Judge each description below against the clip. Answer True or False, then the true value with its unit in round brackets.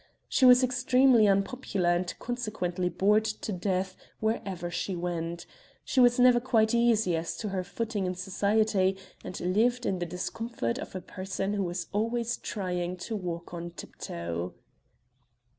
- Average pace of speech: True (150 wpm)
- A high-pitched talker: True (195 Hz)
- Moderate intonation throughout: True (4.3 semitones)